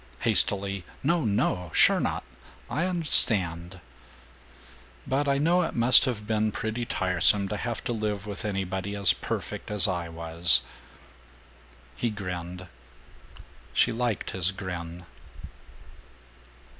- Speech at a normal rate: No, slow, 120 wpm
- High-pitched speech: No, low, 100 Hz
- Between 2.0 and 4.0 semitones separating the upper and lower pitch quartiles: No, average, 4.4 semitones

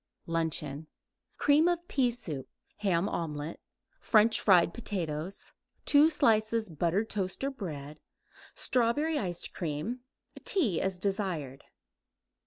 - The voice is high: Yes, high, 195 Hz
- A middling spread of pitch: No, wide, 6.6 semitones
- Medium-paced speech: No, slow, 105 wpm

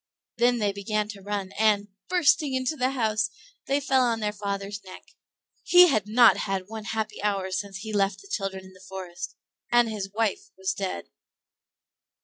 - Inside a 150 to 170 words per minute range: No, average, 180 wpm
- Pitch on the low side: No, high, 215 Hz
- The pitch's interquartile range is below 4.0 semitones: Yes, average, 3.5 semitones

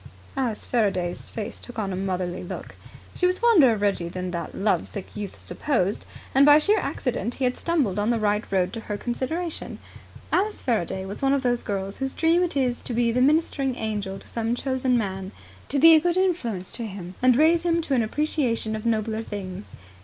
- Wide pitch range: Yes, wide, 5.7 semitones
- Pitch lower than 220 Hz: No, high, 235 Hz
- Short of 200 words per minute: No, fast, 205 wpm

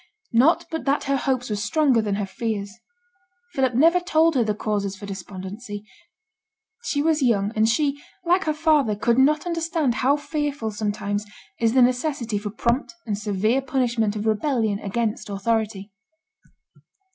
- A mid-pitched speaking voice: No, high, 235 Hz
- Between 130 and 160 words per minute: Yes, average, 155 wpm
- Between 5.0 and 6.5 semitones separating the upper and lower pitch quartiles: Yes, wide, 5.5 semitones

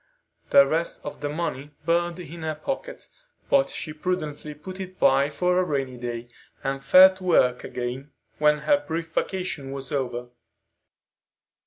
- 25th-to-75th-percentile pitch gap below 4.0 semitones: No, average, 4.9 semitones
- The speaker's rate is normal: Yes, average, 155 wpm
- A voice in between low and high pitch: Yes, medium, 155 Hz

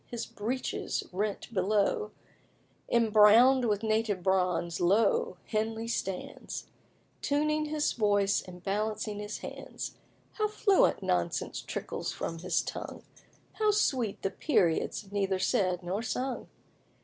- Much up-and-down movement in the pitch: No, average, 3.8 semitones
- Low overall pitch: No, high, 210 Hz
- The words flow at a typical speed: No, slow, 115 wpm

